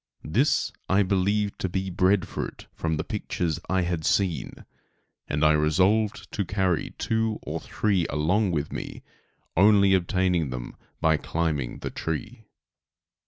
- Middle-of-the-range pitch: No, very low, 95 Hz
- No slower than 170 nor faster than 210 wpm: No, average, 140 wpm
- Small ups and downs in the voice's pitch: No, average, 4.1 semitones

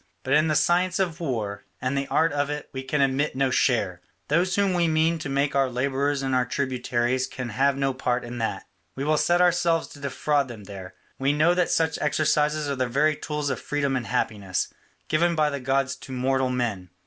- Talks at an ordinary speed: No, fast, 215 wpm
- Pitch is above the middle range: No, medium, 140 Hz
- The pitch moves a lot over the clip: No, average, 3.2 semitones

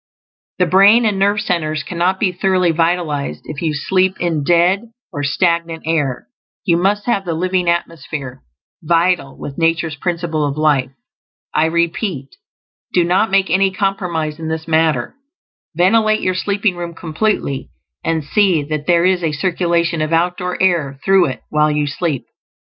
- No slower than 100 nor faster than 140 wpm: No, average, 155 wpm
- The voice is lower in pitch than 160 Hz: No, medium, 170 Hz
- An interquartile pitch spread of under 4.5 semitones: Yes, average, 3.2 semitones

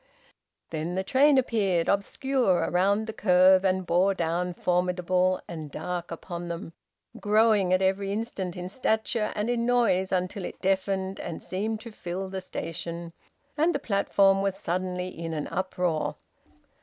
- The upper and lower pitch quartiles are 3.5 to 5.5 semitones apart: No, narrow, 2.6 semitones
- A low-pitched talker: No, high, 190 Hz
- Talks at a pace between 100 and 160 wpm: Yes, average, 150 wpm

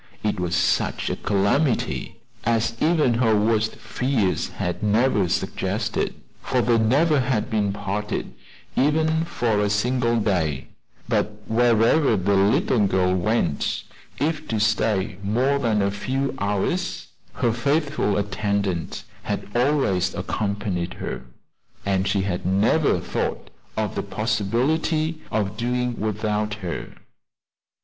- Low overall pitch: Yes, low, 110 Hz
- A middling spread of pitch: Yes, average, 4.0 semitones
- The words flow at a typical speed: No, slow, 125 wpm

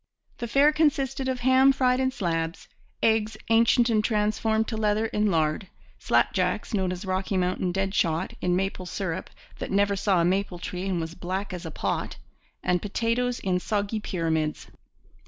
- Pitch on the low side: No, high, 200 Hz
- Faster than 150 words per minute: Yes, average, 170 wpm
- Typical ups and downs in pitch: Yes, average, 4.0 semitones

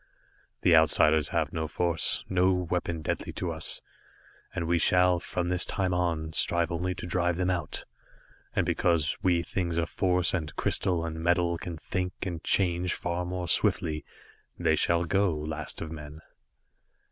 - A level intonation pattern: Yes, narrow, 2.0 semitones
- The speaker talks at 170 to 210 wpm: No, average, 160 wpm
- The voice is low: Yes, very low, 85 Hz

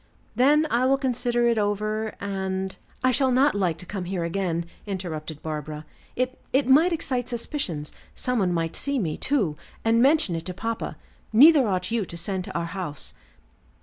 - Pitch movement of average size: No, wide, 6.4 semitones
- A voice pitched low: No, high, 205 Hz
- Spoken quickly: No, average, 180 wpm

